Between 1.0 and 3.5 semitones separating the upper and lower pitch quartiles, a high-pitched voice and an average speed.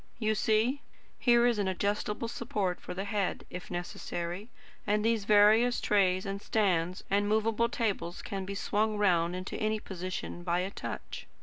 Yes: average, 2.9 semitones; high, 205 Hz; average, 165 wpm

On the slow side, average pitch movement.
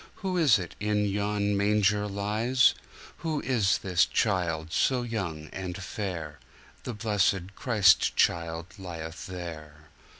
Yes: slow, 110 wpm; average, 3.6 semitones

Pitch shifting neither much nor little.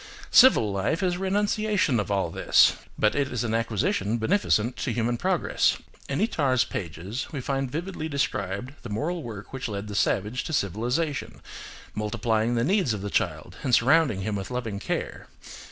No: wide, 5.9 semitones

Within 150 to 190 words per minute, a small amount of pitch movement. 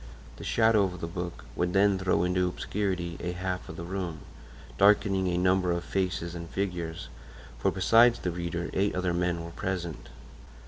Yes: average, 175 wpm; narrow, 1.9 semitones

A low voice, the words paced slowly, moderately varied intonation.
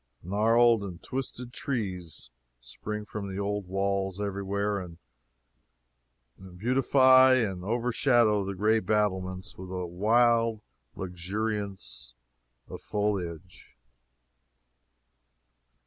Yes: low, 100 Hz; slow, 90 wpm; average, 3.4 semitones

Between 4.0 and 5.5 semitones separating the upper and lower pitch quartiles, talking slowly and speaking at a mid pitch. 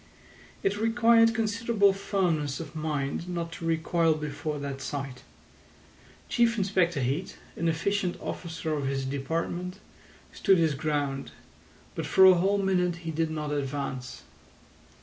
Yes: average, 4.7 semitones; slow, 130 wpm; medium, 165 Hz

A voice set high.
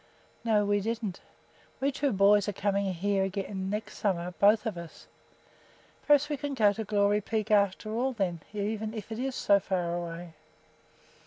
Yes: high, 205 Hz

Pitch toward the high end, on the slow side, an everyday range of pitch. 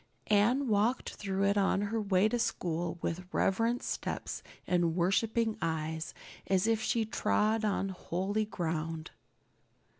Yes: high, 195 Hz; slow, 130 wpm; average, 3.9 semitones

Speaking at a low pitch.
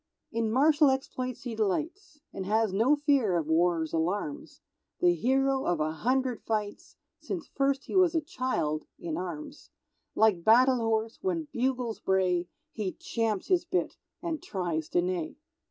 No: high, 230 Hz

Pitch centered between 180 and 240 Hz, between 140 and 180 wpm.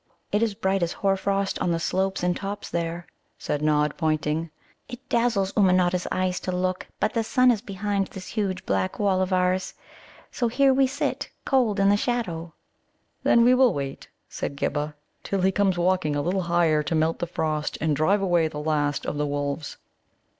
No: medium, 185 Hz; average, 190 wpm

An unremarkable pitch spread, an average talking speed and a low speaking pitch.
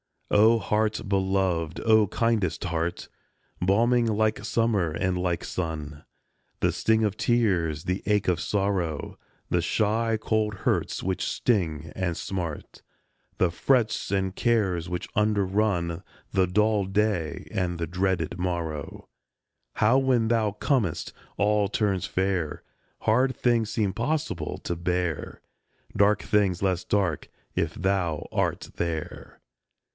No: average, 3.8 semitones; slow, 125 wpm; very low, 95 Hz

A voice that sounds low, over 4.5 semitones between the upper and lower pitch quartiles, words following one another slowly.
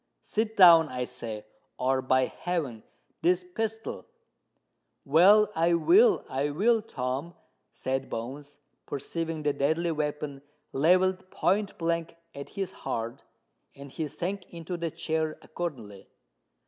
No: medium, 160 Hz; average, 5.0 semitones; slow, 110 wpm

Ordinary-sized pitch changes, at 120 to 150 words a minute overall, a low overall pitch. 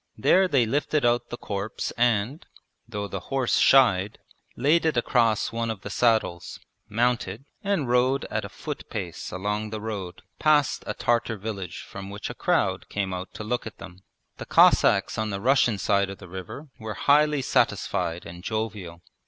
No: average, 4.1 semitones; average, 175 wpm; low, 110 Hz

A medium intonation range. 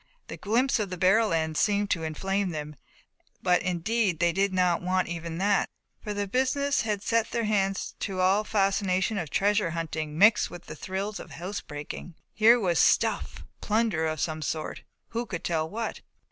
Yes: average, 4.0 semitones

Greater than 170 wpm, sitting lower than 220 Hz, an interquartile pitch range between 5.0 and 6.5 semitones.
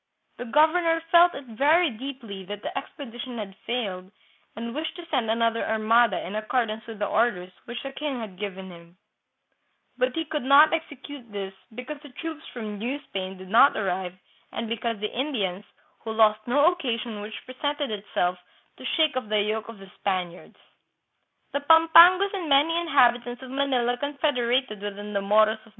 No: average, 180 wpm; high, 235 Hz; wide, 5.4 semitones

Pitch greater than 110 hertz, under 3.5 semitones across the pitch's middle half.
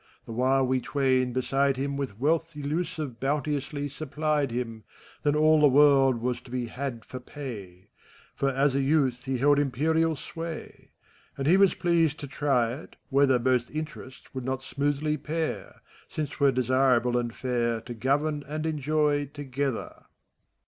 Yes: medium, 140 Hz; average, 2.8 semitones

